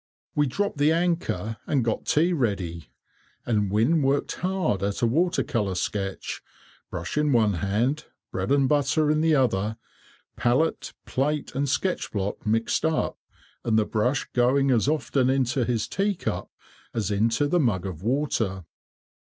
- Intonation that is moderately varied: No, wide, 6.0 semitones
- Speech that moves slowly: No, average, 150 wpm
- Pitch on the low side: Yes, low, 125 Hz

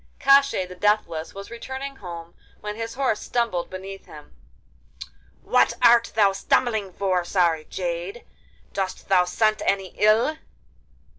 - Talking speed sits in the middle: No, slow, 130 wpm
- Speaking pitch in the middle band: No, high, 200 Hz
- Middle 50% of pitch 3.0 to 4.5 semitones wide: Yes, average, 4.2 semitones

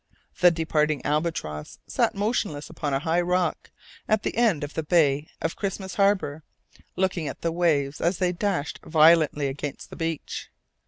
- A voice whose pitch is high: No, medium, 165 Hz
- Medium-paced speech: Yes, average, 160 wpm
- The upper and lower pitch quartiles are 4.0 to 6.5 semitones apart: No, average, 3.6 semitones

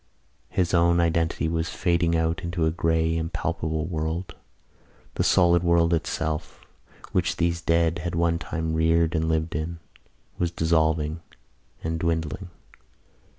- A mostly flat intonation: Yes, narrow, 1.0 semitones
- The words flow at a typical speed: No, slow, 130 wpm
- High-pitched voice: No, very low, 85 Hz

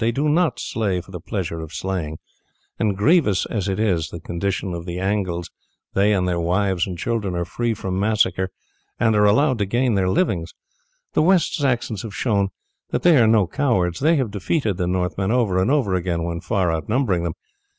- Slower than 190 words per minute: No, average, 195 wpm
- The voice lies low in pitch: Yes, low, 100 Hz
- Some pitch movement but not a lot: Yes, average, 4.3 semitones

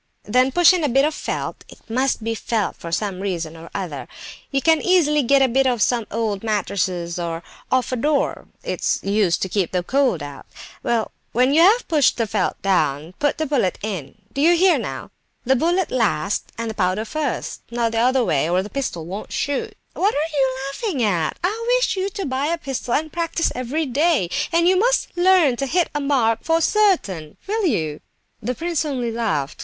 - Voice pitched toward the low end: No, very high, 255 Hz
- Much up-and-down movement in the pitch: Yes, wide, 7.9 semitones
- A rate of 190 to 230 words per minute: Yes, fast, 205 wpm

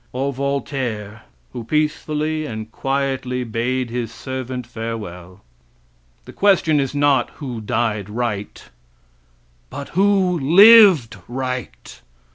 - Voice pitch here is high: No, low, 130 Hz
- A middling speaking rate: No, slow, 100 wpm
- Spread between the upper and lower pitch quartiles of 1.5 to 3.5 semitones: No, average, 4.2 semitones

